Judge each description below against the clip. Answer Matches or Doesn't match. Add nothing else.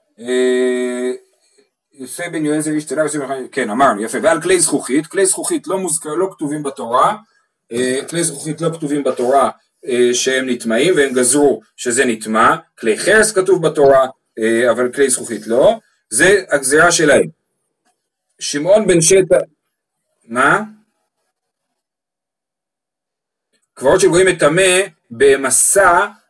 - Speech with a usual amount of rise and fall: Doesn't match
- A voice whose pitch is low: Doesn't match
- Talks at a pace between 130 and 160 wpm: Doesn't match